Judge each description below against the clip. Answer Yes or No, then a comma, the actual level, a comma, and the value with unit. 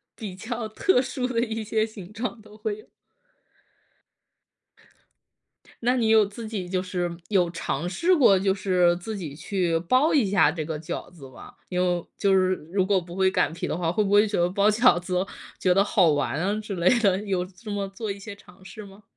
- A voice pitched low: No, high, 195 Hz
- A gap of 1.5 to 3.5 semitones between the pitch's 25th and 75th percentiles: Yes, average, 3.2 semitones